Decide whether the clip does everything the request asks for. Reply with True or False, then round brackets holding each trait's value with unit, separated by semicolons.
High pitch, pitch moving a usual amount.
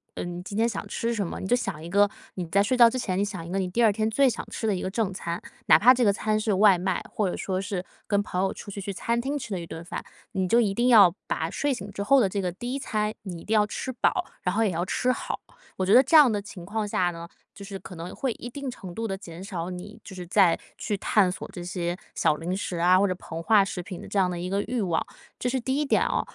True (200 Hz; 3.8 semitones)